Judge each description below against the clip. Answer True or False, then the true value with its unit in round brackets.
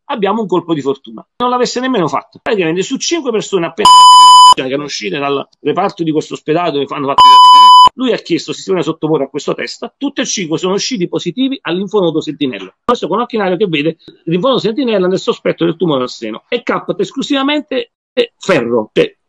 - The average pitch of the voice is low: False (200 Hz)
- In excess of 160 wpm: True (170 wpm)